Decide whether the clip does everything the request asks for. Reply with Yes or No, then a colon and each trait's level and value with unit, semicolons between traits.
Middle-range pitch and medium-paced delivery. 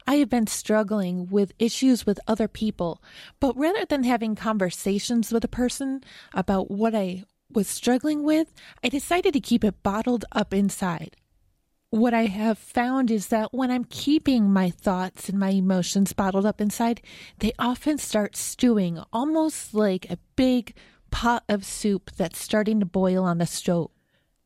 No: high, 215 Hz; average, 160 wpm